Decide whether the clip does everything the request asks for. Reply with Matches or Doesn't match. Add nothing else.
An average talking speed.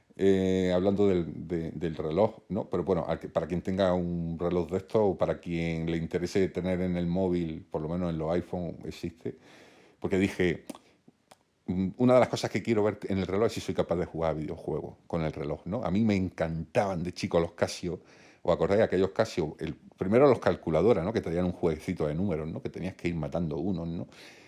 Doesn't match